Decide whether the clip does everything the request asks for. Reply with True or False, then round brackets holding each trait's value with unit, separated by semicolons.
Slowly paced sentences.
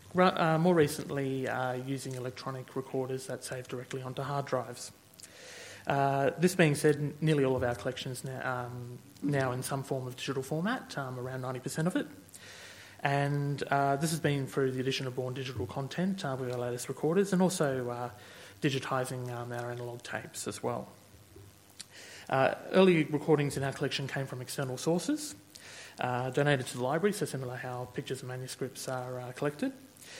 False (180 wpm)